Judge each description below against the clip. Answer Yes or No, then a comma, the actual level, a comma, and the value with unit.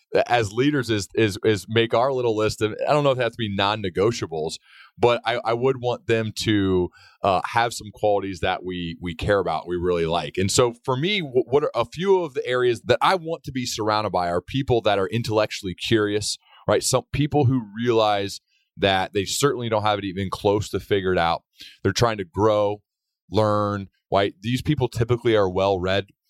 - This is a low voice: Yes, low, 110 Hz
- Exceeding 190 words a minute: Yes, fast, 205 wpm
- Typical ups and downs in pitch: Yes, average, 3.8 semitones